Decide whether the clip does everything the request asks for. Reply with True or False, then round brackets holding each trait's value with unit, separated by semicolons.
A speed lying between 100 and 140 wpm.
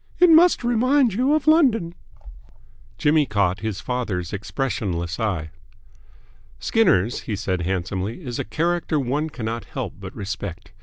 True (135 wpm)